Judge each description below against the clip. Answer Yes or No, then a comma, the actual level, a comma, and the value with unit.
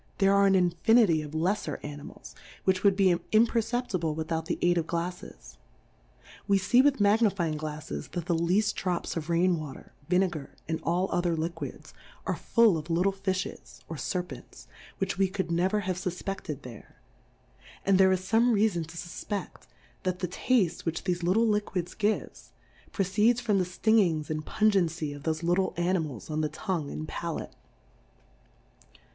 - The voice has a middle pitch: Yes, medium, 180 Hz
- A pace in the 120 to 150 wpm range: No, average, 165 wpm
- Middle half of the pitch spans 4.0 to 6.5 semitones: No, average, 3.3 semitones